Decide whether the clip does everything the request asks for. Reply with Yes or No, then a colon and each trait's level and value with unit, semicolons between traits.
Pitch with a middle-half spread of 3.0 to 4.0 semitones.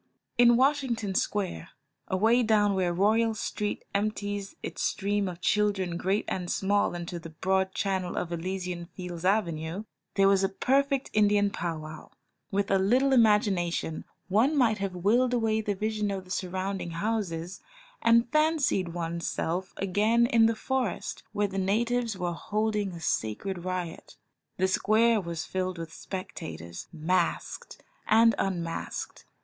Yes: average, 3.5 semitones